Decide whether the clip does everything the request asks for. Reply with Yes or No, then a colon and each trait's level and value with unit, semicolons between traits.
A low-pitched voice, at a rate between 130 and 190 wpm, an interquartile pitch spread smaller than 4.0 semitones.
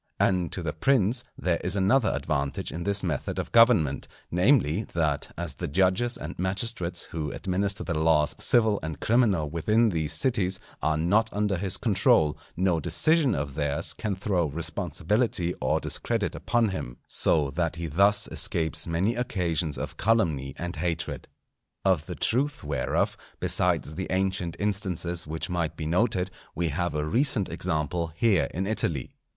No: very low, 90 Hz; average, 155 wpm; average, 4.4 semitones